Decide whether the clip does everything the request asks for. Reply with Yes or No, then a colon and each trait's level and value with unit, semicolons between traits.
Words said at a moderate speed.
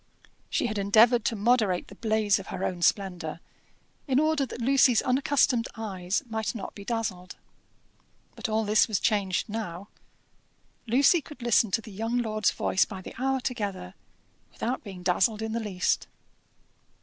Yes: average, 160 wpm